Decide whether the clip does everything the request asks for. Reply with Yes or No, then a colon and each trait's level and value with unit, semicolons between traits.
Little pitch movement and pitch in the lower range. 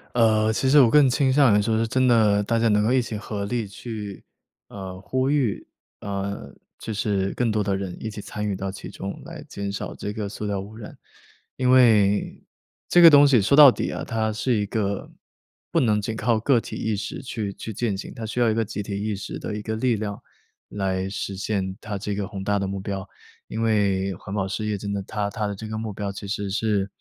Yes: narrow, 2.3 semitones; low, 105 Hz